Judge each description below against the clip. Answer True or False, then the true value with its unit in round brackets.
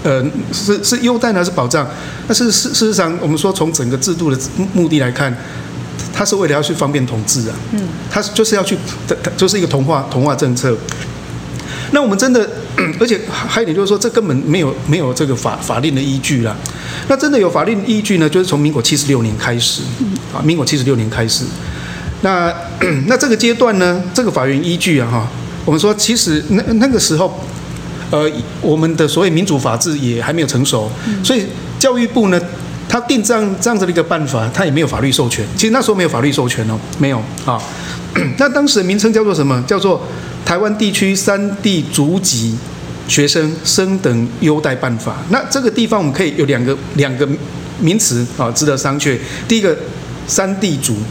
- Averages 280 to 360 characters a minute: True (300 characters per minute)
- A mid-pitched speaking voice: True (155 Hz)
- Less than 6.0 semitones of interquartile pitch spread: False (7.3 semitones)